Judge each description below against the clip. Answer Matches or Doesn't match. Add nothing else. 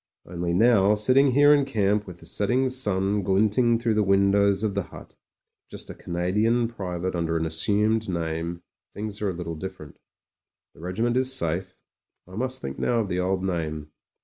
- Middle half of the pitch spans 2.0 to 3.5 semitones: Doesn't match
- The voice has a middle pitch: Doesn't match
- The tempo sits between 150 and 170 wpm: Doesn't match